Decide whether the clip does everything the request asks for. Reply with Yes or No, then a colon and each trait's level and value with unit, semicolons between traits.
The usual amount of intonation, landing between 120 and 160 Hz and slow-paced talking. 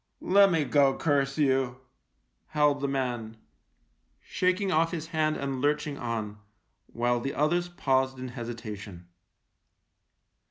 Yes: average, 4.1 semitones; low, 135 Hz; slow, 125 wpm